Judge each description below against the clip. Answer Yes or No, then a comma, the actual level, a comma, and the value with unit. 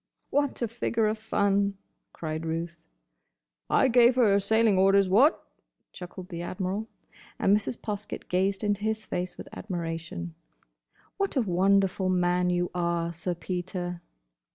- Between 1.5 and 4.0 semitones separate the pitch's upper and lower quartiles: Yes, average, 3.2 semitones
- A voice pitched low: No, high, 190 Hz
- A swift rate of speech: No, slow, 135 wpm